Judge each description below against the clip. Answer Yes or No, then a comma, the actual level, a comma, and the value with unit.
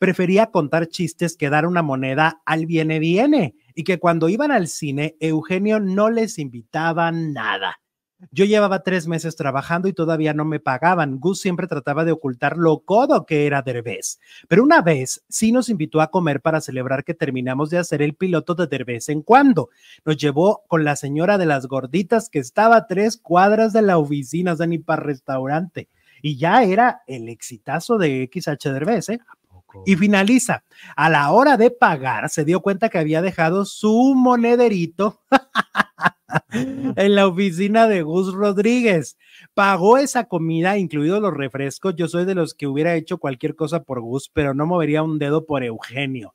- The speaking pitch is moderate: Yes, medium, 165 Hz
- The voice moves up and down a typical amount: Yes, average, 4.7 semitones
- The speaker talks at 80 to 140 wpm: No, fast, 170 wpm